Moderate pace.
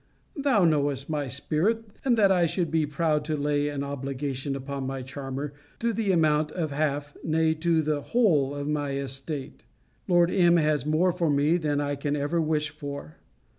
Yes: average, 180 wpm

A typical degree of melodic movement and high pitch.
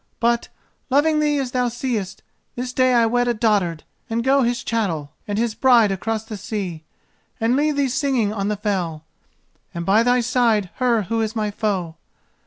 Yes: average, 3.4 semitones; high, 225 Hz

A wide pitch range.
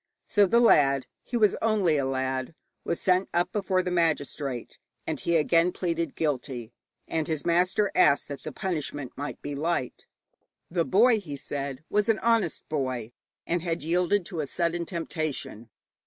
No: average, 4.5 semitones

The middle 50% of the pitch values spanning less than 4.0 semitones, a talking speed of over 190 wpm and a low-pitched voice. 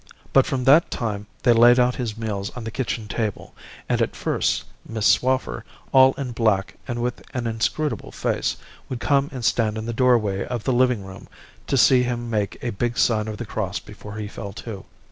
Yes: average, 2.8 semitones; average, 200 wpm; low, 115 Hz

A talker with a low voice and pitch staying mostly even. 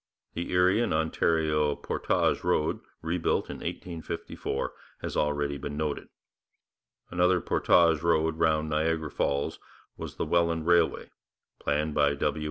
Yes: very low, 80 Hz; narrow, 2.1 semitones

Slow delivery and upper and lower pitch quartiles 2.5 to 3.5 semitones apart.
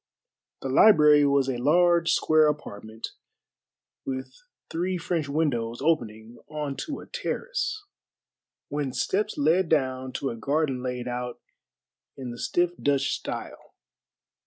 No: slow, 125 wpm; average, 4.8 semitones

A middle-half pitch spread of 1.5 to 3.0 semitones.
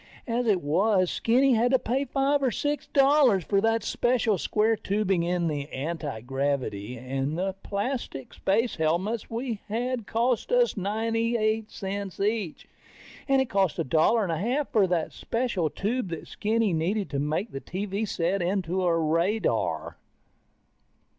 No: wide, 5.4 semitones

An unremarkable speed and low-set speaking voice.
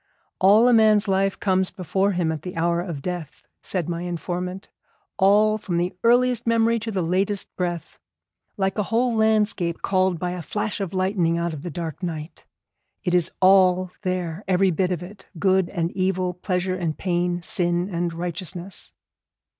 No: average, 170 wpm; medium, 185 Hz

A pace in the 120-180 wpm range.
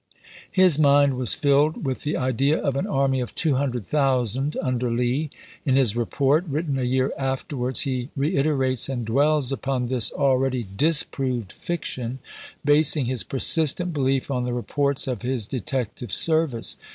Yes: average, 150 wpm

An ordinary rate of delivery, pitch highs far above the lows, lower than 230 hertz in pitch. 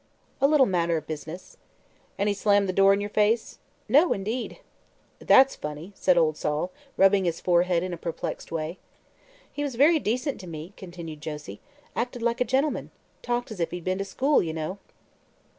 Yes: average, 185 wpm; wide, 6.1 semitones; high, 190 Hz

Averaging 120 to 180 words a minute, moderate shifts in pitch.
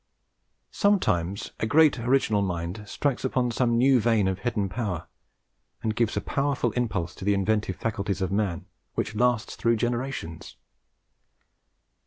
Yes: average, 140 wpm; average, 4.0 semitones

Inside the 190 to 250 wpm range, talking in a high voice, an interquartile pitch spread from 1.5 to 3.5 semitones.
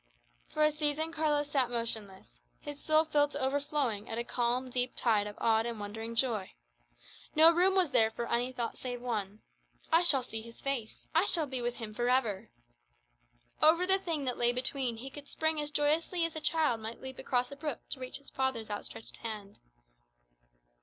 No: average, 195 wpm; very high, 255 Hz; average, 4.6 semitones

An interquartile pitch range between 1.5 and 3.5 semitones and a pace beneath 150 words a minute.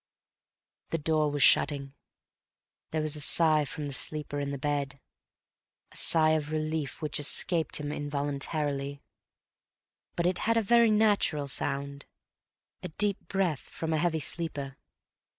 Yes: narrow, 2.5 semitones; slow, 135 wpm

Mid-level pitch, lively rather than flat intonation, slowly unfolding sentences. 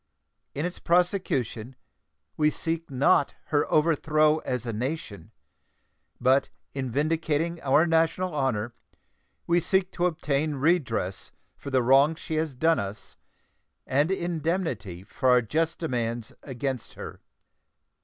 No: medium, 145 Hz; average, 4.5 semitones; slow, 125 wpm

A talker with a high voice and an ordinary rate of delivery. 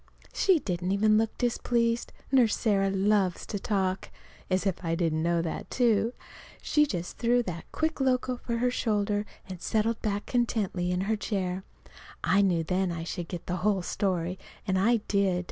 Yes: high, 200 Hz; average, 180 wpm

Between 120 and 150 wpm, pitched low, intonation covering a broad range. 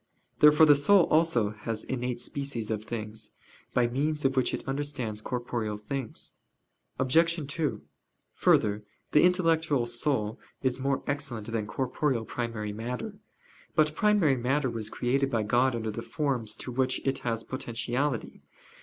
No: average, 145 wpm; low, 125 Hz; average, 4.1 semitones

